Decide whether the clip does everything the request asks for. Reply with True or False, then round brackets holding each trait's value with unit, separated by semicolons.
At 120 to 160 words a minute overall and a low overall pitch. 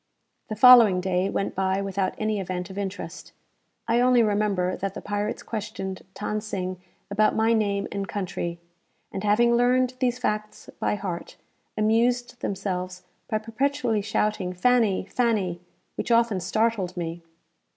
False (140 wpm; 205 Hz)